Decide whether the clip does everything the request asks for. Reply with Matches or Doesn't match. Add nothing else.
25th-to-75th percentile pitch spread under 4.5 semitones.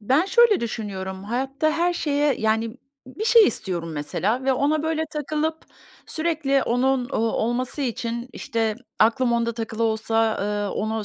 Doesn't match